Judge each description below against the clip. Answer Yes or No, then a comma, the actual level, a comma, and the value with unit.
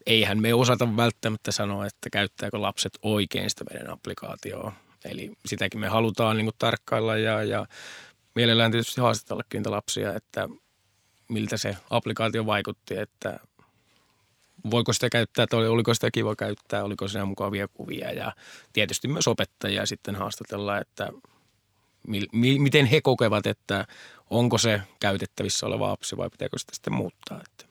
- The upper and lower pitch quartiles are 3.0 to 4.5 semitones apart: No, narrow, 2.4 semitones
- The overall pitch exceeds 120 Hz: No, low, 110 Hz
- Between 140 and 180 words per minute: Yes, average, 145 wpm